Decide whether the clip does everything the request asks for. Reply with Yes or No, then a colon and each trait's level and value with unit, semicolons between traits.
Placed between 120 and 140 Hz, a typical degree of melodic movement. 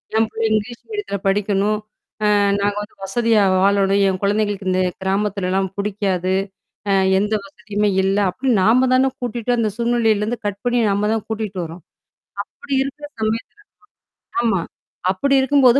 No: high, 210 Hz; average, 3.1 semitones